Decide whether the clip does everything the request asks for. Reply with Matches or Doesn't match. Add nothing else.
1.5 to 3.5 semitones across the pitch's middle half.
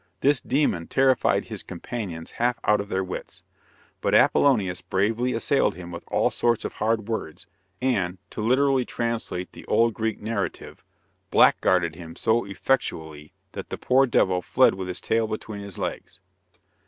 Doesn't match